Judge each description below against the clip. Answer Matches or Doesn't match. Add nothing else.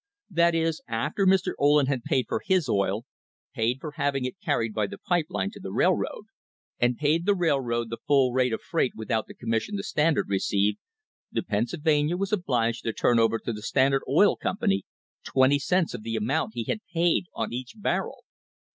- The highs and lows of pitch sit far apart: Matches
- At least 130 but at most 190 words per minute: Doesn't match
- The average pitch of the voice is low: Matches